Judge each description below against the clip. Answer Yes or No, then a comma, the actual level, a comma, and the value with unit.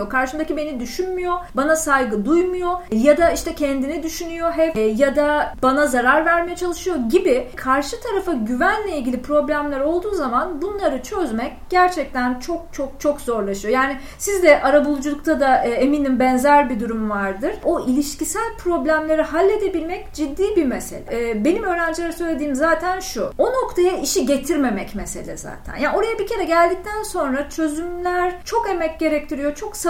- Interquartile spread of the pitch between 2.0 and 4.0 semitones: No, average, 4.6 semitones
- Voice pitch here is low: No, very high, 315 Hz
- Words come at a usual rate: Yes, average, 150 wpm